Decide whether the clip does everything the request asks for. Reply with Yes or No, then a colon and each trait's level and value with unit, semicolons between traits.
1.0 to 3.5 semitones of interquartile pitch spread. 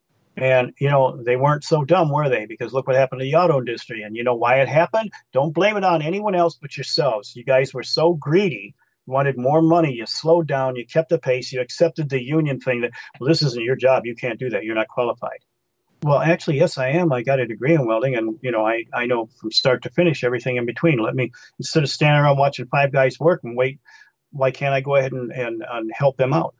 No: average, 4.5 semitones